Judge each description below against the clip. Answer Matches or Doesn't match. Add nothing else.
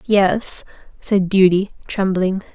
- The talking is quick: Doesn't match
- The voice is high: Matches